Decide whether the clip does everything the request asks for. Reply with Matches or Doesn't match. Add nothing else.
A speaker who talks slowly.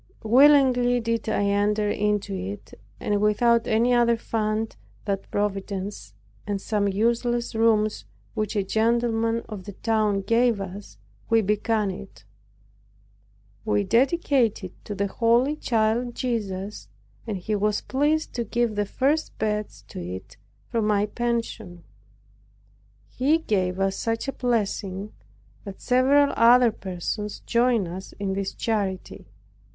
Matches